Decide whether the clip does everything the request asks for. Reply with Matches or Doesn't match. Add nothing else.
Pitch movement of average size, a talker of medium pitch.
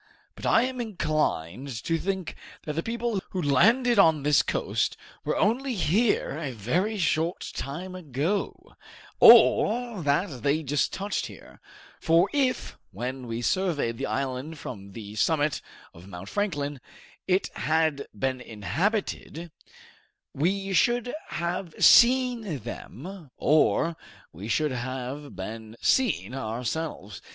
Doesn't match